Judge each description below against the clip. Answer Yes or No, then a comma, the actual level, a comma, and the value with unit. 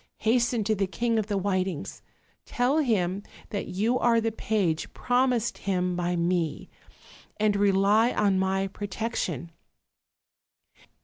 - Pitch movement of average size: Yes, average, 3.5 semitones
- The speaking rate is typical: No, slow, 125 wpm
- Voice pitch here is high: Yes, high, 200 Hz